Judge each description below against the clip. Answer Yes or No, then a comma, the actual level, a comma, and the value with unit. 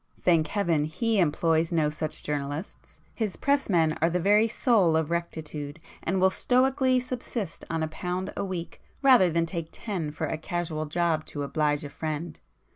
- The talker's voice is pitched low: No, medium, 170 Hz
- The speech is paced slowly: No, average, 170 wpm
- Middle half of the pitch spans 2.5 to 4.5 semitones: Yes, average, 4.1 semitones